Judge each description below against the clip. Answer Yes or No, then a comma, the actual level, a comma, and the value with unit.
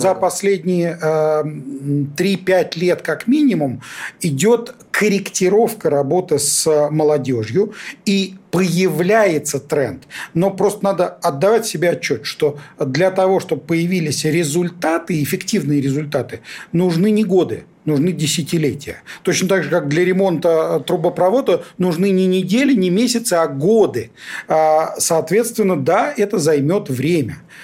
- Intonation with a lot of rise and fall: No, average, 3.8 semitones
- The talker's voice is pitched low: No, medium, 175 Hz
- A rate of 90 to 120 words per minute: Yes, average, 115 wpm